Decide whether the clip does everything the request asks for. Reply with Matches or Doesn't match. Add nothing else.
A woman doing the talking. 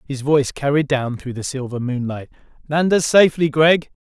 Doesn't match